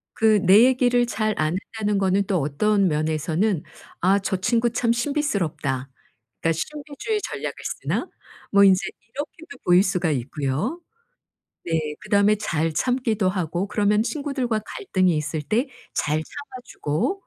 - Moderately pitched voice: No, high, 200 Hz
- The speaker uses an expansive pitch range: Yes, wide, 6.7 semitones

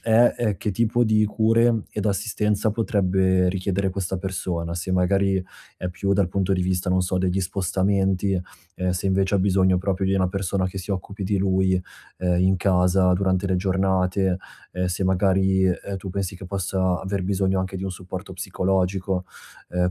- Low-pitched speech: Yes, very low, 95 Hz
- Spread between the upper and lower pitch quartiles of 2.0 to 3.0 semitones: No, narrow, 1.2 semitones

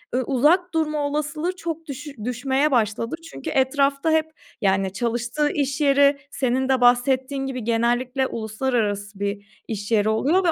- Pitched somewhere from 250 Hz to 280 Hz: Yes, very high, 265 Hz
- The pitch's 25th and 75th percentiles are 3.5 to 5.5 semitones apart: Yes, average, 4.2 semitones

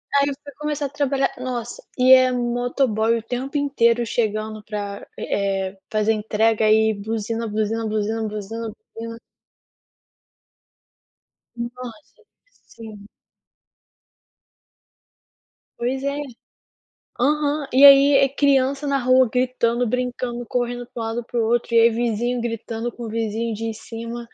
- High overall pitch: Yes, high, 235 Hz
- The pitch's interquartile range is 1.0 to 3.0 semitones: Yes, narrow, 2.6 semitones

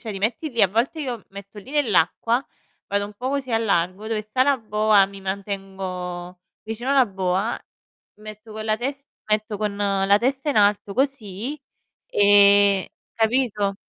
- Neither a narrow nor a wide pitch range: Yes, average, 3.2 semitones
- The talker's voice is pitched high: Yes, high, 210 Hz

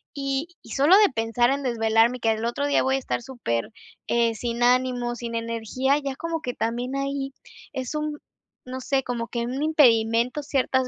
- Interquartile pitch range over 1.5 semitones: Yes, average, 2.9 semitones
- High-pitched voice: Yes, very high, 250 Hz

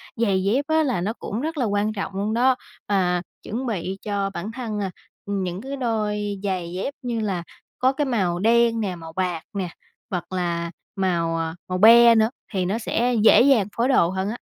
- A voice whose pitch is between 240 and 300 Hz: No, high, 205 Hz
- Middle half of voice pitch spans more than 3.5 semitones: Yes, average, 4.2 semitones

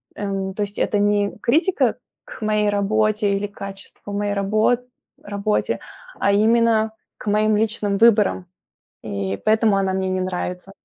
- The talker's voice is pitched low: No, high, 205 Hz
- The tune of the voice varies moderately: No, narrow, 1.5 semitones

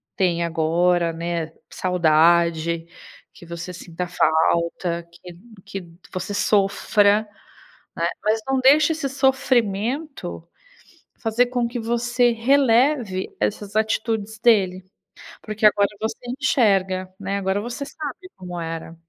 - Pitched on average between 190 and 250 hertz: Yes, high, 200 Hz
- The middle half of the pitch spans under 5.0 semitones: No, wide, 5.5 semitones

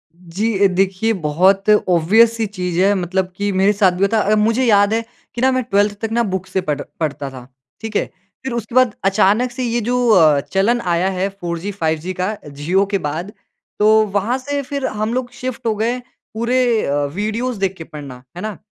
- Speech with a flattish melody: No, average, 4.2 semitones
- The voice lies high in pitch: Yes, high, 205 Hz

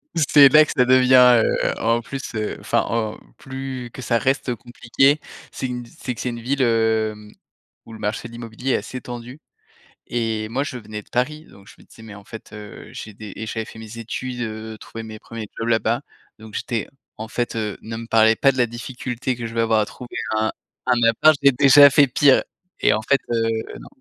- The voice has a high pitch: No, low, 115 Hz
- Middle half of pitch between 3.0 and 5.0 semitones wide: No, narrow, 2.5 semitones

